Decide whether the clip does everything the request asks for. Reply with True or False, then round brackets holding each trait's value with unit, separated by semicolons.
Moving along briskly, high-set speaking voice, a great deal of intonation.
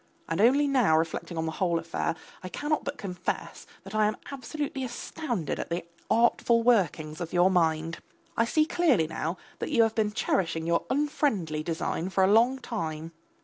False (180 wpm; 195 Hz; 6.8 semitones)